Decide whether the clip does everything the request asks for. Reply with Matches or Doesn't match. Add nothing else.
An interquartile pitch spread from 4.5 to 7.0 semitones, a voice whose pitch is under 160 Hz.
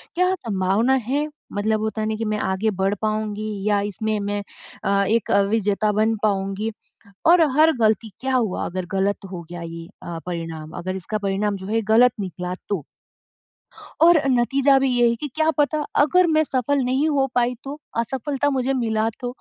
Doesn't match